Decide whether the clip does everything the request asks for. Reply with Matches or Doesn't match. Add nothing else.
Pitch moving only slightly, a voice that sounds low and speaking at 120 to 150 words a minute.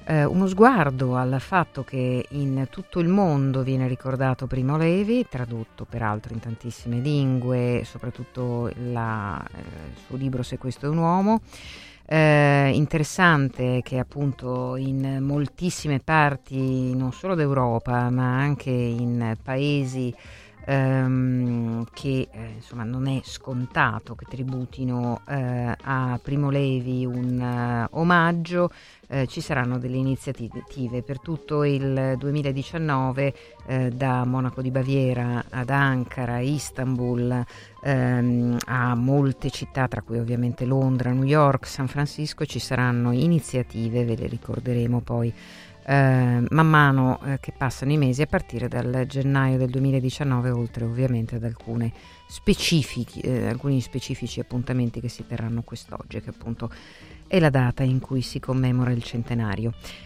Matches